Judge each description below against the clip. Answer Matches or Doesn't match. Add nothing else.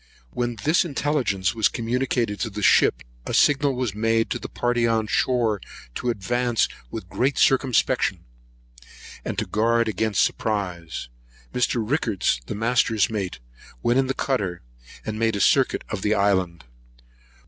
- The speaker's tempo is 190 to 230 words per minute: Doesn't match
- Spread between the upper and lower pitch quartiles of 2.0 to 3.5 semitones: Matches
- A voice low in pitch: Matches